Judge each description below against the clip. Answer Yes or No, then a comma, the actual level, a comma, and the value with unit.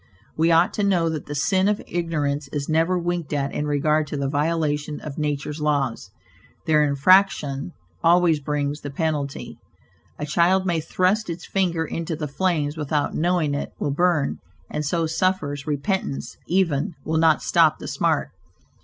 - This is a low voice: No, medium, 155 Hz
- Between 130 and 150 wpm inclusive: No, average, 160 wpm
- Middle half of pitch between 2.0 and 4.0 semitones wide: Yes, average, 3.1 semitones